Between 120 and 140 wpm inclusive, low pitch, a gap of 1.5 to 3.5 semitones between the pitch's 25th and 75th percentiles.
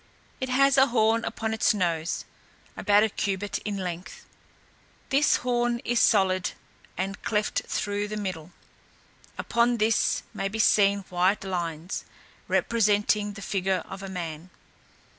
No: slow, 135 wpm; high, 205 Hz; average, 3.0 semitones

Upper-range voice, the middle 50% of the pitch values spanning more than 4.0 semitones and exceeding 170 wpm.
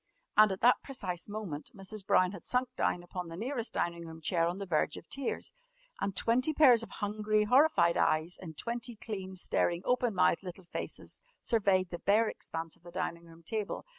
Yes: high, 195 Hz; average, 4.9 semitones; average, 195 wpm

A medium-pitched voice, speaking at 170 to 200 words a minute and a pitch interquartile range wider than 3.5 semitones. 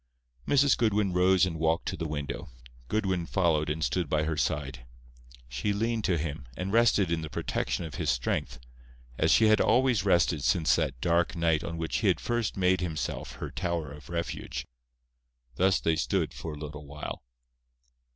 No: very low, 85 Hz; average, 180 wpm; average, 3.9 semitones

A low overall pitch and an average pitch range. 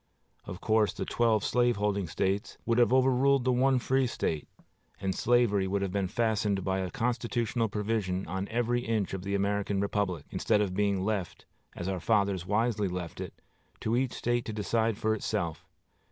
Yes: low, 105 Hz; average, 3.4 semitones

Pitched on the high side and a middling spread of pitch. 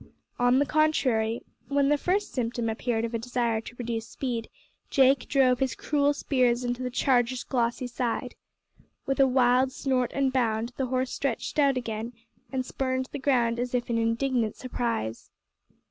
No: very high, 250 Hz; narrow, 2.2 semitones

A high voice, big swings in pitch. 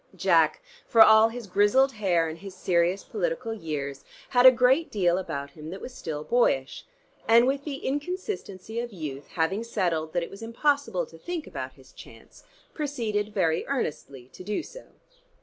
Yes: high, 210 Hz; wide, 7.3 semitones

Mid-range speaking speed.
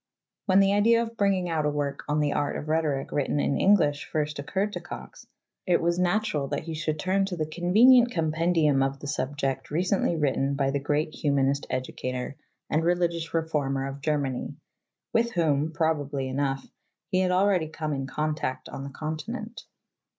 Yes: average, 180 wpm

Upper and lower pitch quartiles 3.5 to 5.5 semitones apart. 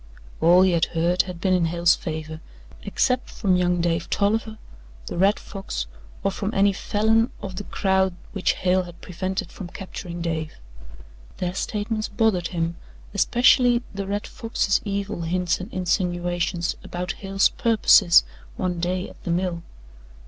No: narrow, 2.6 semitones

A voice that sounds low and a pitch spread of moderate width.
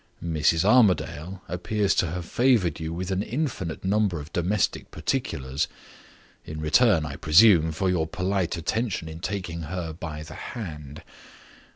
Yes: very low, 90 Hz; average, 3.9 semitones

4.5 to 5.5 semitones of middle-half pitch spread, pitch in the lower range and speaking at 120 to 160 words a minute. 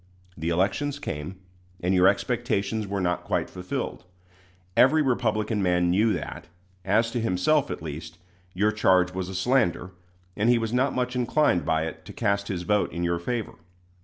No: average, 5.1 semitones; low, 100 Hz; average, 170 wpm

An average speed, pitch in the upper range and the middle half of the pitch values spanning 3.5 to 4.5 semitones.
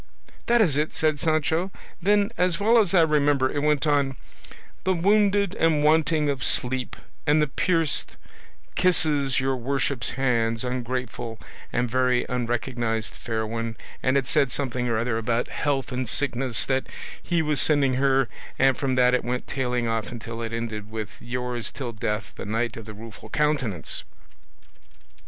No: average, 165 wpm; low, 130 Hz; average, 4.2 semitones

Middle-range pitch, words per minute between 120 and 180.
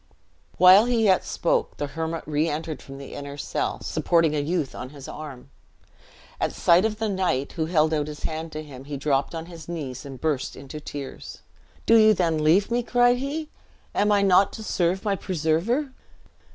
No: medium, 165 Hz; average, 190 wpm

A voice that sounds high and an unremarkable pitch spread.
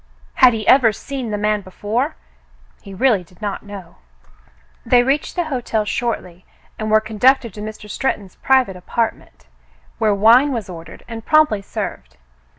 Yes: high, 215 Hz; average, 3.9 semitones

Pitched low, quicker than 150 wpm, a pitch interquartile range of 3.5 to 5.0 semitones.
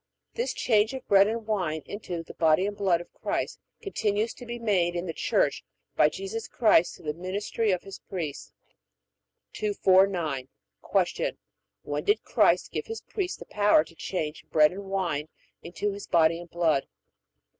No: high, 190 Hz; average, 165 wpm; average, 4.1 semitones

